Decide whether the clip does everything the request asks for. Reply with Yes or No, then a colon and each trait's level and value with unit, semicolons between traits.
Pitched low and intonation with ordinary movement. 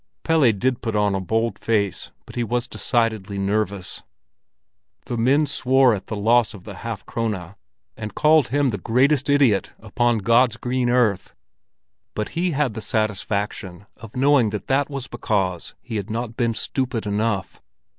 Yes: low, 115 Hz; average, 3.7 semitones